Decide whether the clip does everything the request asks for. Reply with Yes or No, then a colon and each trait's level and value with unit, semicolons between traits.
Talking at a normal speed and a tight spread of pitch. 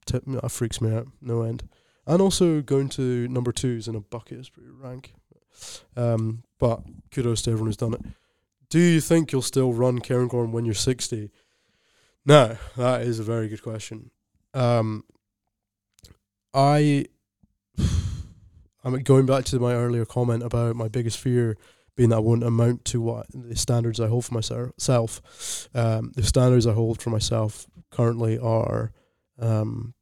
Yes: average, 160 wpm; narrow, 2.2 semitones